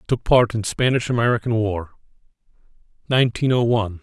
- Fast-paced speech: No, slow, 135 wpm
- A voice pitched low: Yes, low, 115 Hz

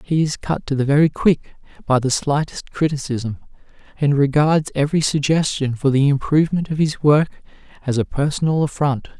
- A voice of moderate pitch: Yes, medium, 145 Hz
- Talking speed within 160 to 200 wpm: Yes, average, 165 wpm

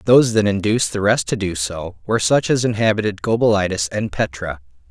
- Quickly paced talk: No, average, 185 wpm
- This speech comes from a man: Yes, male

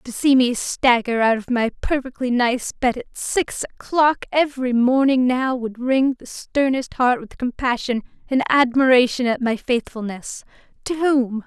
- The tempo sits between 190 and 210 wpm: No, average, 150 wpm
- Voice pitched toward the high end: Yes, very high, 250 Hz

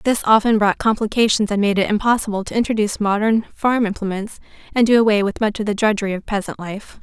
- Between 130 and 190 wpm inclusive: No, fast, 205 wpm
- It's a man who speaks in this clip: No, female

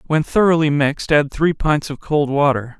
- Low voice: No, medium, 145 Hz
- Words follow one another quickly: No, average, 195 wpm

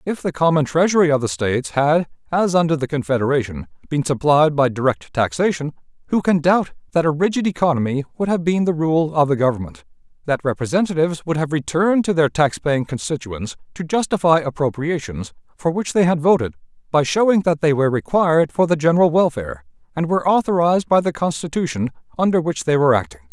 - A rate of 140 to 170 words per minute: No, average, 185 wpm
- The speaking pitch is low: No, medium, 155 Hz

